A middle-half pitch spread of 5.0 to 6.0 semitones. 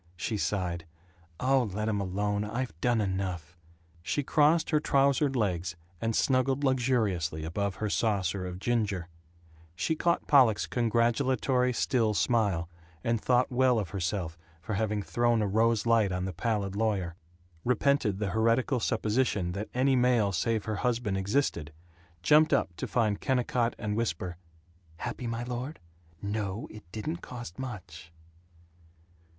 No: average, 4.4 semitones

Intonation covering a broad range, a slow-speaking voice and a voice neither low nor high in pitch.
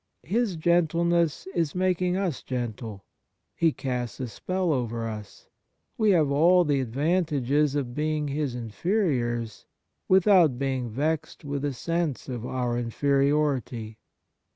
Yes: wide, 5.7 semitones; slow, 125 wpm; medium, 145 Hz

